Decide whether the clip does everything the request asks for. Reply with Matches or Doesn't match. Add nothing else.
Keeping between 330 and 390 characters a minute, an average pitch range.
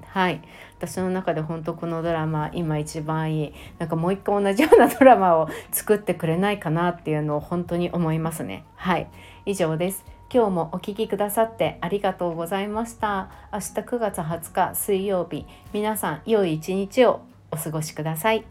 Matches